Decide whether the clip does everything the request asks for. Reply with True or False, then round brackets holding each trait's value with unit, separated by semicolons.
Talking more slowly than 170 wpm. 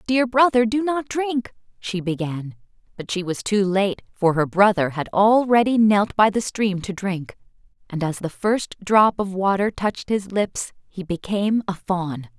False (180 wpm)